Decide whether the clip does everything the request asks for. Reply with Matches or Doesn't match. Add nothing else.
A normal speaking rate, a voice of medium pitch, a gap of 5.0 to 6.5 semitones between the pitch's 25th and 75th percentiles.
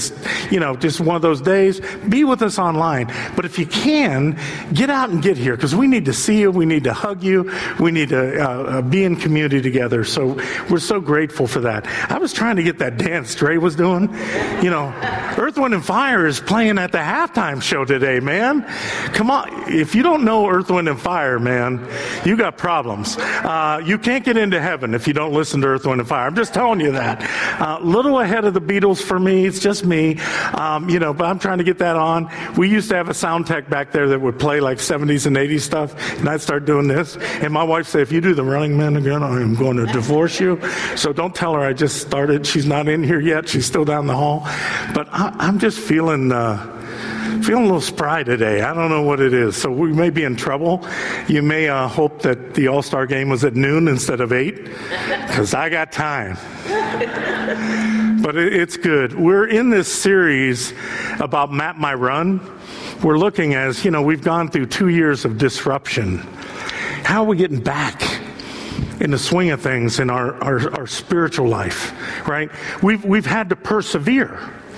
Doesn't match